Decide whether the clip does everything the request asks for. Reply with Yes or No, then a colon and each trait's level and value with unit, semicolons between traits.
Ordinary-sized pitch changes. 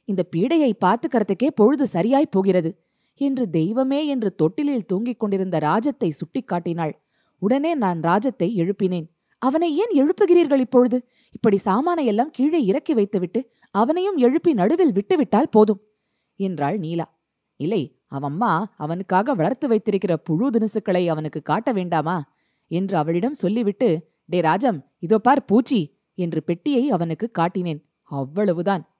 No: wide, 6.7 semitones